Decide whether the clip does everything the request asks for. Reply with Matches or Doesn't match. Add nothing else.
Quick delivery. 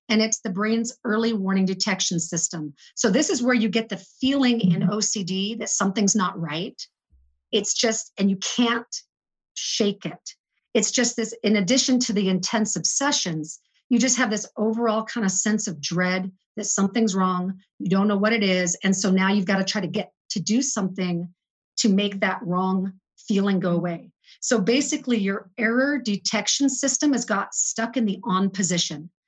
Doesn't match